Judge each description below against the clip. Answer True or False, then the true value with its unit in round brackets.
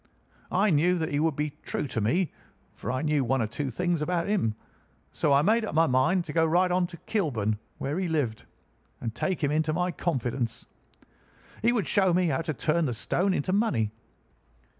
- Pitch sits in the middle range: True (155 Hz)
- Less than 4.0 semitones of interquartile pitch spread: False (5.3 semitones)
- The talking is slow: False (205 wpm)